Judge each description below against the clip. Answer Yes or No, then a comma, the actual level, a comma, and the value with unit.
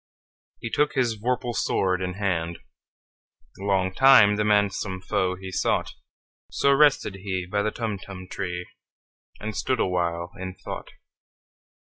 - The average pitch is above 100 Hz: No, very low, 95 Hz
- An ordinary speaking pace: No, slow, 115 wpm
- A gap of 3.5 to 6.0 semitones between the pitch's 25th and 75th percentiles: No, average, 2.9 semitones